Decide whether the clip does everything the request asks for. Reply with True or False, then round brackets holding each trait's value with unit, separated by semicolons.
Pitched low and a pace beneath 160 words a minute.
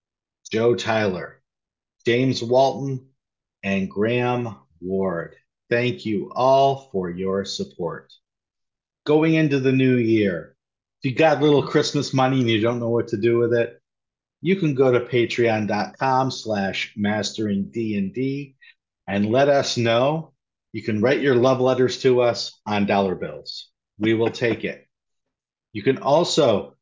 True (120 Hz; 140 wpm)